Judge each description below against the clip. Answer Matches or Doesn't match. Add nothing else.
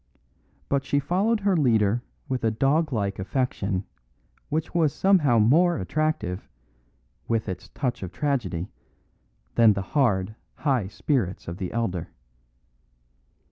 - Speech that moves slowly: Matches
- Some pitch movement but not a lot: Doesn't match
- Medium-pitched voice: Doesn't match